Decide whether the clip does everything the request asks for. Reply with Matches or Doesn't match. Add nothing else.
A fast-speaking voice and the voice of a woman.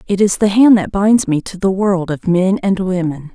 Matches